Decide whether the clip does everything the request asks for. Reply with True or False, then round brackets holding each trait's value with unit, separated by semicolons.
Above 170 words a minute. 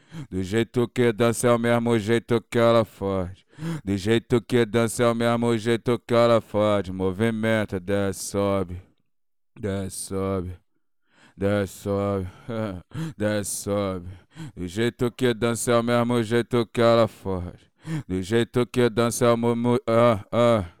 False (145 wpm)